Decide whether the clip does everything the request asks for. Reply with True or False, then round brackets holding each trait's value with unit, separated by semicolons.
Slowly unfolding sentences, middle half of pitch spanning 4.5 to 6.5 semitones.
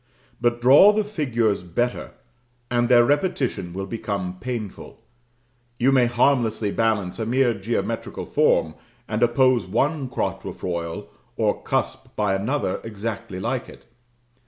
False (125 wpm; 4.0 semitones)